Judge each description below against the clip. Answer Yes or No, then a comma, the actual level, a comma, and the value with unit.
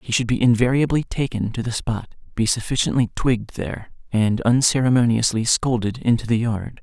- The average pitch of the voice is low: Yes, low, 115 Hz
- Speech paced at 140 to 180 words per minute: Yes, average, 160 wpm